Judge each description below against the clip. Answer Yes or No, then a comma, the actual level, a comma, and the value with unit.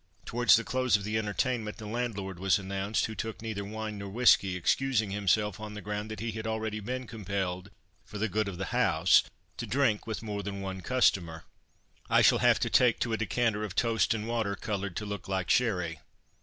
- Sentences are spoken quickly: Yes, fast, 210 wpm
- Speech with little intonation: Yes, narrow, 2.3 semitones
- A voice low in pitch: Yes, low, 105 Hz